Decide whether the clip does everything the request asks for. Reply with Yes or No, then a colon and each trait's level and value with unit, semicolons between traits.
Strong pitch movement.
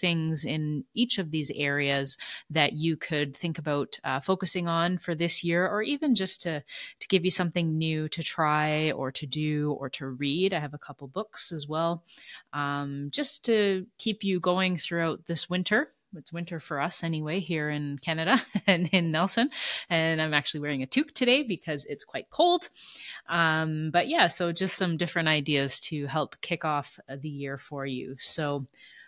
No: average, 3.7 semitones